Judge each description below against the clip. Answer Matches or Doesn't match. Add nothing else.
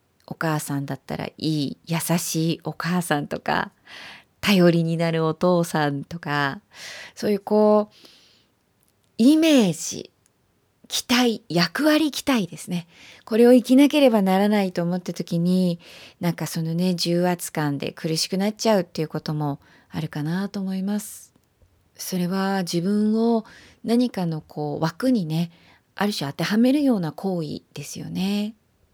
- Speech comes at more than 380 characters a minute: Doesn't match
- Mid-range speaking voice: Matches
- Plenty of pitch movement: Doesn't match